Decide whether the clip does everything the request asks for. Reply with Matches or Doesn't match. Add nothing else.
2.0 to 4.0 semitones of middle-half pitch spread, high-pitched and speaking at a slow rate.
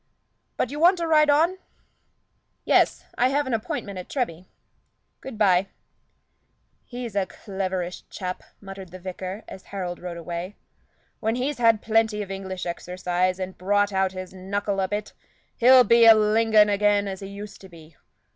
Doesn't match